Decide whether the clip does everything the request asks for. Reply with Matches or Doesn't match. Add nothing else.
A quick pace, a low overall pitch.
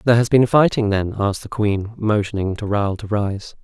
Matches